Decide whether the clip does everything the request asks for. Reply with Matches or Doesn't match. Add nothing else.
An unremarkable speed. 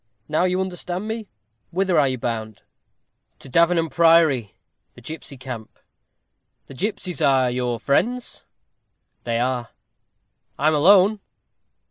Doesn't match